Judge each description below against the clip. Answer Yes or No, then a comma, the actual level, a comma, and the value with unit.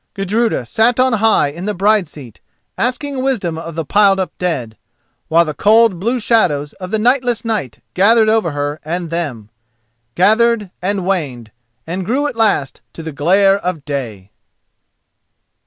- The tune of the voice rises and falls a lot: Yes, wide, 7.1 semitones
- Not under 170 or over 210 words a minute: No, average, 155 wpm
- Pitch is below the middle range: No, medium, 185 Hz